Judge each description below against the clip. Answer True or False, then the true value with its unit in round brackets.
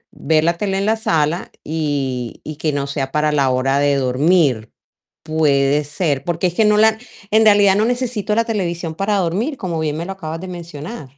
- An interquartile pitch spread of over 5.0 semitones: True (5.5 semitones)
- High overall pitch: False (165 Hz)